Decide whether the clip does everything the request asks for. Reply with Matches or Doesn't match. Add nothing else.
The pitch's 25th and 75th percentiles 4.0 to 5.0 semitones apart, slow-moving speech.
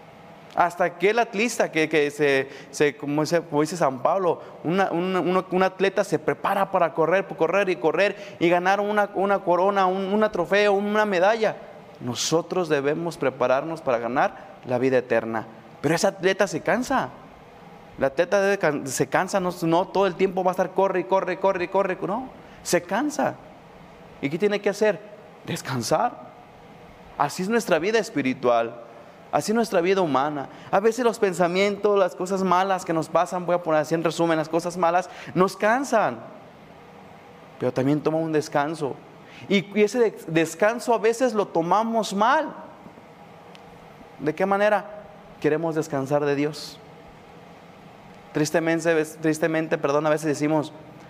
Doesn't match